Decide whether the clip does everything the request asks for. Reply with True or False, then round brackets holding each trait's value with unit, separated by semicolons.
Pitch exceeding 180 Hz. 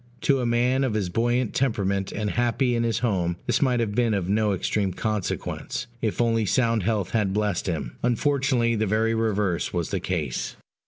False (110 Hz)